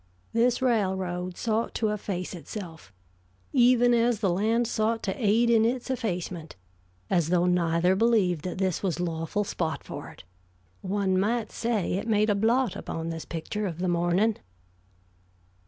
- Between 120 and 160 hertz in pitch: No, high, 200 Hz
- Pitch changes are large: No, average, 4.4 semitones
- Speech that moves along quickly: No, average, 155 wpm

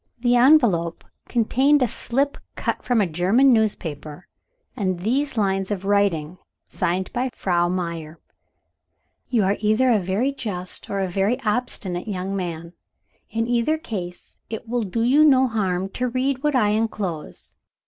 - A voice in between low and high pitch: No, high, 210 Hz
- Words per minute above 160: No, average, 150 wpm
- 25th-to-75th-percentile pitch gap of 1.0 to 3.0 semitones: No, average, 5.2 semitones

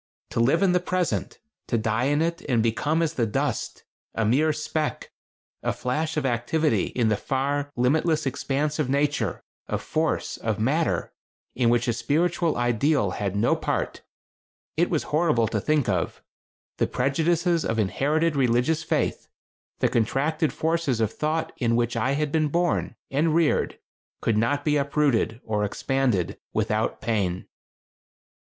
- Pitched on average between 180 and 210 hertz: No, medium, 140 Hz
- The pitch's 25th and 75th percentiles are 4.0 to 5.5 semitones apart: Yes, average, 5.2 semitones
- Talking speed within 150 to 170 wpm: Yes, average, 155 wpm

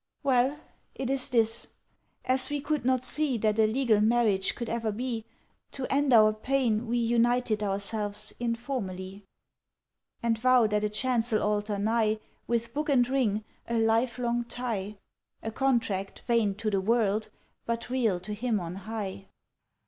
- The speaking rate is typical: Yes, average, 150 wpm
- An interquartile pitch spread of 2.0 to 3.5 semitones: Yes, average, 2.8 semitones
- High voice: Yes, high, 230 Hz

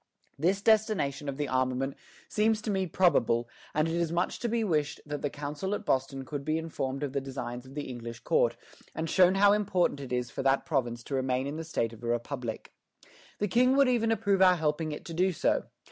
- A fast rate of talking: Yes, fast, 220 wpm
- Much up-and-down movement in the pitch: Yes, wide, 6.2 semitones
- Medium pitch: Yes, medium, 150 Hz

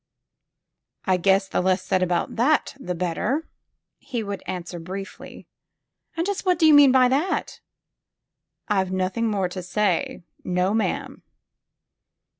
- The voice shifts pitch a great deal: Yes, wide, 5.9 semitones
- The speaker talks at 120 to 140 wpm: Yes, slow, 135 wpm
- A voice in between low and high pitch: No, high, 195 Hz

